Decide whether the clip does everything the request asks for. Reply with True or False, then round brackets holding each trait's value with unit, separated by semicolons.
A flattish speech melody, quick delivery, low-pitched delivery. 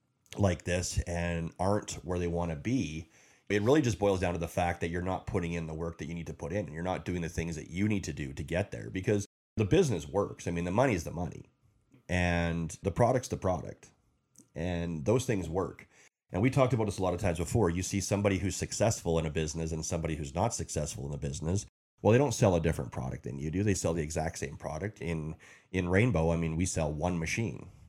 False (3.6 semitones; 245 wpm; 90 Hz)